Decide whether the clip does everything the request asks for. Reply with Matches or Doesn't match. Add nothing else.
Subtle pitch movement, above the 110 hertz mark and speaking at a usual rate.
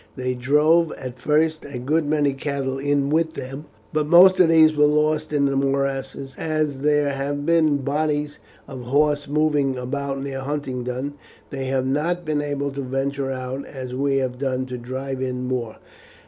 Matches